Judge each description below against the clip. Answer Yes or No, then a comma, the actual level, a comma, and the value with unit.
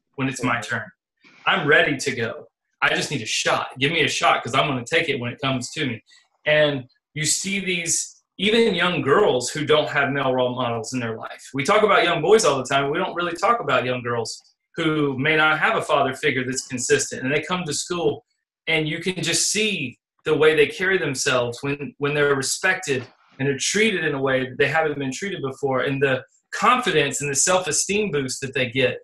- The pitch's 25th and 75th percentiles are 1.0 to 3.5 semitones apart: No, average, 4.4 semitones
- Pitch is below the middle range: No, medium, 145 Hz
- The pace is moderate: No, fast, 230 wpm